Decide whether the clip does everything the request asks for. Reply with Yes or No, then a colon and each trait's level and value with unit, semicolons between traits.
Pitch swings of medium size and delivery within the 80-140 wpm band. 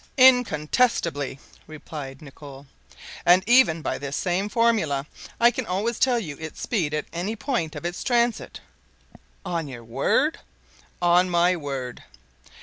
No: wide, 7.8 semitones; slow, 135 wpm